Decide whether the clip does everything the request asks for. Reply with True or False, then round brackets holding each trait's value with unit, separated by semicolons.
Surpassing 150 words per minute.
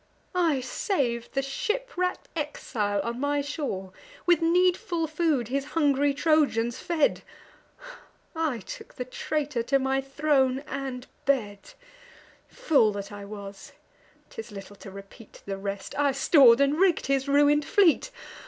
False (135 wpm)